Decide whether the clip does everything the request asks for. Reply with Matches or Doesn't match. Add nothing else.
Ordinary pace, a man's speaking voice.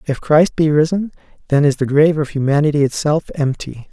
Matches